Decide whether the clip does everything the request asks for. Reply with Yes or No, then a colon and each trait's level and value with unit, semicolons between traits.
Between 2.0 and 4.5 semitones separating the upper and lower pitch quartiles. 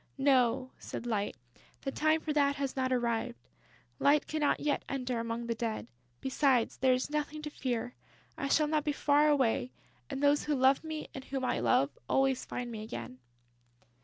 Yes: average, 3.5 semitones